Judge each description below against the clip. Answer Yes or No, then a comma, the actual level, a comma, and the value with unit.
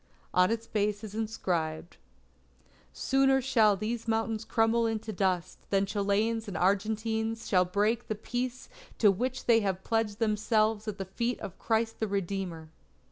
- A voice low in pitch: No, high, 215 Hz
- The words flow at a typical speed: Yes, average, 150 wpm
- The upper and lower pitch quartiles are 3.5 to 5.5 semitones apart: No, narrow, 2.5 semitones